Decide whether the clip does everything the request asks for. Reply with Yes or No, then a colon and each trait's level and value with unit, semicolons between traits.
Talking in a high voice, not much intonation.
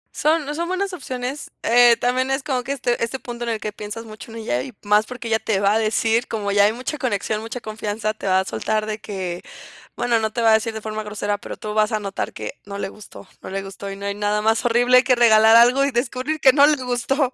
No: high, 225 Hz; average, 3.1 semitones